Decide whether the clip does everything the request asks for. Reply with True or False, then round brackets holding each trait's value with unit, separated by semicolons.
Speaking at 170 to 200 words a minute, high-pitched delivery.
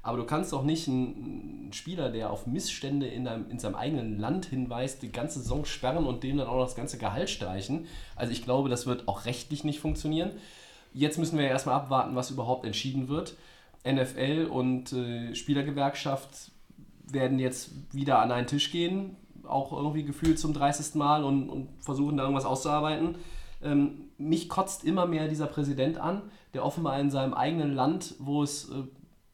False (180 wpm; 140 Hz)